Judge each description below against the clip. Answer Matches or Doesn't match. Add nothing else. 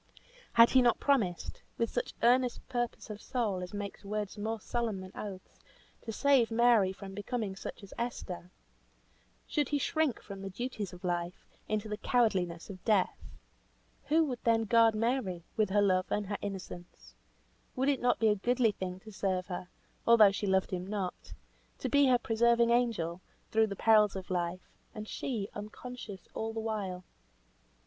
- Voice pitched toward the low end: Doesn't match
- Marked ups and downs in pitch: Doesn't match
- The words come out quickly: Doesn't match